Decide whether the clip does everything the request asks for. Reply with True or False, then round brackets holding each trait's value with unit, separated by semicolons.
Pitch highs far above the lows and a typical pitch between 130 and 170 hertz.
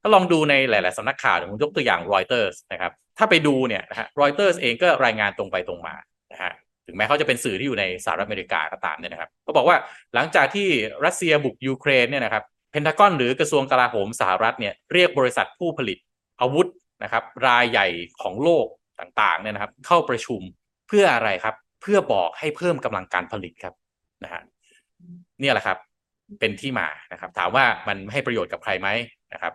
True (8.5 semitones; 140 Hz)